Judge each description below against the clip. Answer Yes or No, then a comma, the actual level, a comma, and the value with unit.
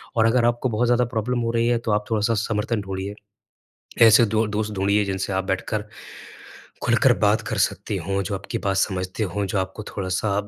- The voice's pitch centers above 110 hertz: No, low, 105 Hz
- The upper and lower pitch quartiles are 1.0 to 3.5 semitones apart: Yes, average, 2.7 semitones